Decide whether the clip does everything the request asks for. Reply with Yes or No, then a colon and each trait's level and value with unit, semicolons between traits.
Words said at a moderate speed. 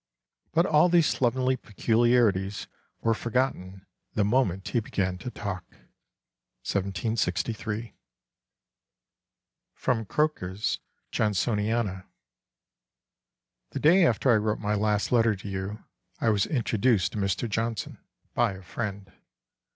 No: slow, 110 wpm